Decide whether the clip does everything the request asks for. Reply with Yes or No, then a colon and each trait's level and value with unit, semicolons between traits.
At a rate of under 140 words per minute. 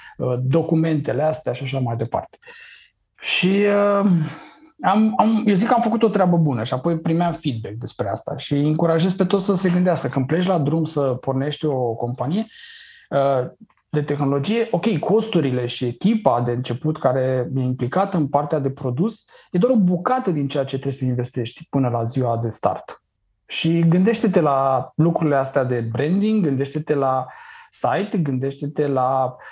No: average, 165 wpm